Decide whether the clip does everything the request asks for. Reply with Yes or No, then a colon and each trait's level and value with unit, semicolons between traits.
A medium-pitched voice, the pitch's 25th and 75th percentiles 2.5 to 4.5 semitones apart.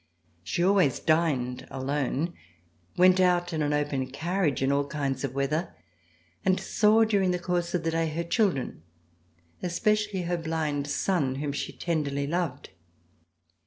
Yes: medium, 160 Hz; average, 4.2 semitones